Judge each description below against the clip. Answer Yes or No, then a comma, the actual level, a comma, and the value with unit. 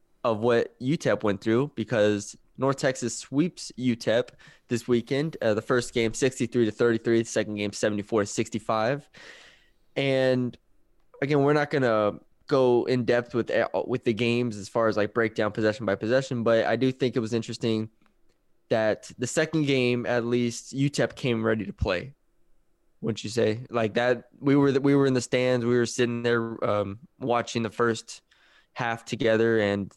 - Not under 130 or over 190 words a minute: Yes, average, 175 wpm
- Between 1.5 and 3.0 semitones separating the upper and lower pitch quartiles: Yes, narrow, 2.4 semitones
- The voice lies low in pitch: Yes, low, 120 Hz